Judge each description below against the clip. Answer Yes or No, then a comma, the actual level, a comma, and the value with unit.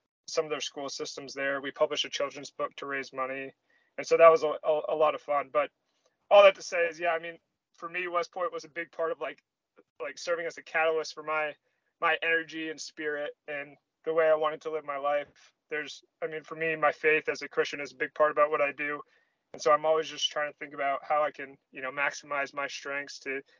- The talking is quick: Yes, fast, 250 wpm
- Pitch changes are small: Yes, narrow, 2.2 semitones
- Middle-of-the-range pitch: Yes, medium, 150 Hz